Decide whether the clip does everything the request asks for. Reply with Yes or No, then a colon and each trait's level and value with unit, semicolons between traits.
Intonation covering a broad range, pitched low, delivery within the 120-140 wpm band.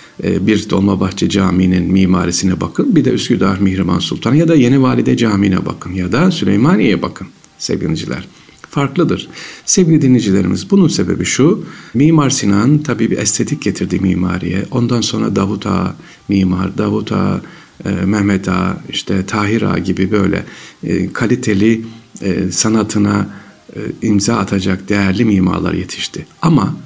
No: average, 3.4 semitones; low, 100 Hz; average, 125 wpm